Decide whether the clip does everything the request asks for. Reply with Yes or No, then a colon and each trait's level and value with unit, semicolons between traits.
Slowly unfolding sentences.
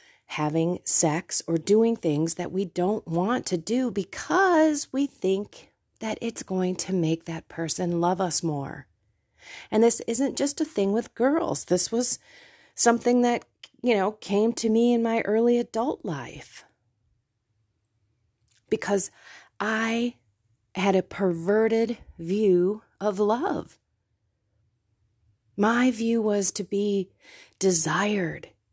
Yes: slow, 125 wpm